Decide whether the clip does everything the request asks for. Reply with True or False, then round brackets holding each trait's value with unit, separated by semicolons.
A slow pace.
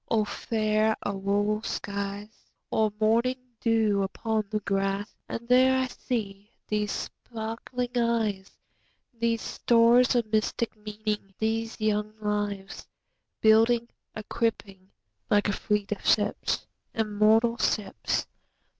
True (90 wpm)